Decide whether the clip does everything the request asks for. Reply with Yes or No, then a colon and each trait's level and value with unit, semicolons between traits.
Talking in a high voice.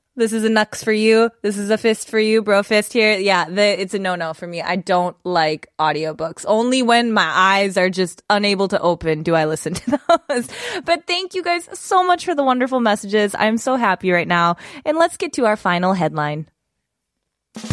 Yes: high, 210 Hz